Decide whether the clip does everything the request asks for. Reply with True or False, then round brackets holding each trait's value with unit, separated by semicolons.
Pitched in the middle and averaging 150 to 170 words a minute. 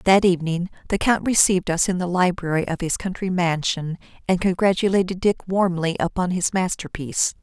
True (180 Hz; 160 wpm)